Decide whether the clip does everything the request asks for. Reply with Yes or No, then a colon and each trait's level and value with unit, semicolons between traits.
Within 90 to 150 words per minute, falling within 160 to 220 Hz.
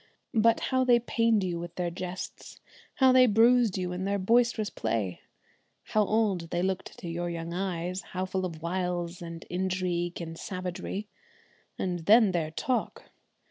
No: average, 160 wpm; medium, 185 Hz